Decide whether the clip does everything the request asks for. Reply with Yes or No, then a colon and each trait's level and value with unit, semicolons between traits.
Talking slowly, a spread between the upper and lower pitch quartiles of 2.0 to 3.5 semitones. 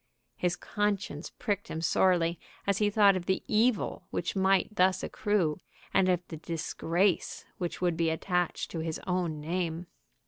No: average, 160 wpm; average, 2.9 semitones